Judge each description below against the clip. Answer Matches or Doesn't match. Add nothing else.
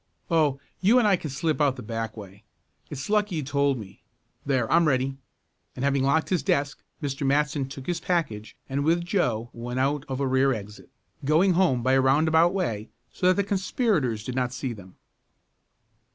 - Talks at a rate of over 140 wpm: Matches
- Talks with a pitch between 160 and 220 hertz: Doesn't match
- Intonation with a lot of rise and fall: Doesn't match